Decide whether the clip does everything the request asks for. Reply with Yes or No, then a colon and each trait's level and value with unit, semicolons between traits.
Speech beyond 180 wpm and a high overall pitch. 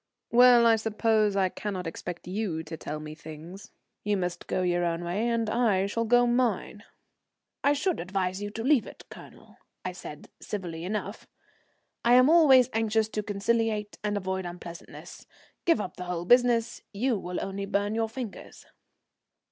No: average, 165 wpm; high, 205 Hz